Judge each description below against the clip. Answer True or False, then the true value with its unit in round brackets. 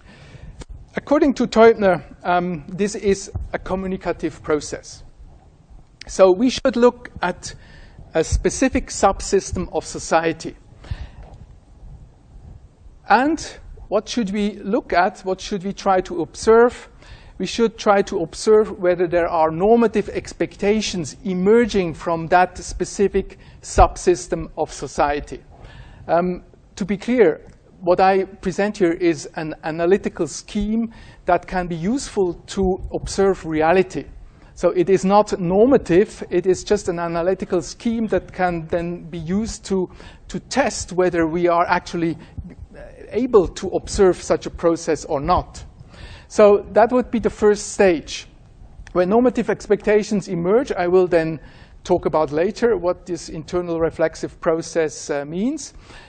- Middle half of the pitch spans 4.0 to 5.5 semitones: False (3.4 semitones)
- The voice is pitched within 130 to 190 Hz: True (185 Hz)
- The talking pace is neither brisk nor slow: False (130 wpm)